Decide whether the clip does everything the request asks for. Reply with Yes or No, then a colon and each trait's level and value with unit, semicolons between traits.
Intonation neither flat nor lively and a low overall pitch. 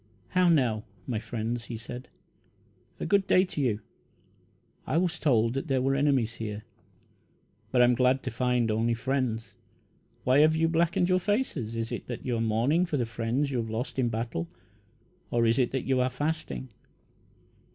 Yes: average, 4.4 semitones; low, 125 Hz